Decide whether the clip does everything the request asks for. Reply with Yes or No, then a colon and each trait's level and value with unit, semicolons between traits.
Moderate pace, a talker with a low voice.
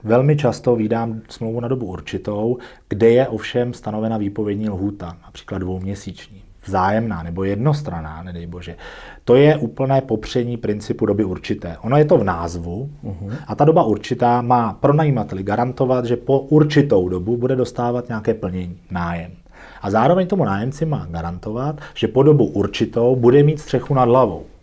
Yes: average, 155 wpm; low, 115 Hz